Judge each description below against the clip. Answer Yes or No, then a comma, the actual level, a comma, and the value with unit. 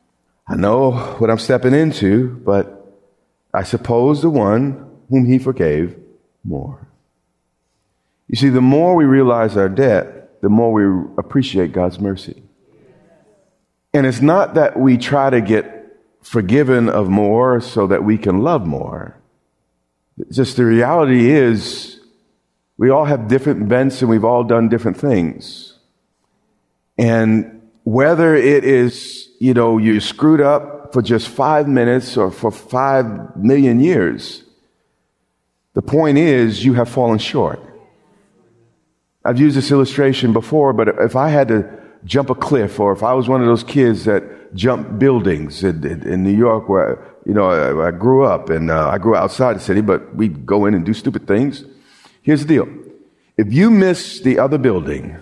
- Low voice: Yes, low, 120 Hz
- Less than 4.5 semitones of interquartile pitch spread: No, average, 4.8 semitones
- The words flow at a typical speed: Yes, average, 160 wpm